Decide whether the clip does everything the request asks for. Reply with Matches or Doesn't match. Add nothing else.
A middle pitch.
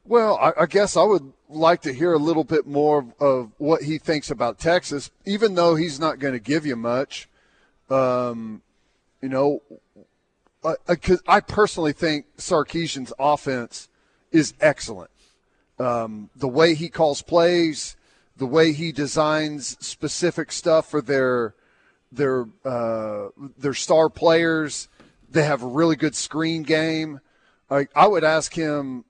Matches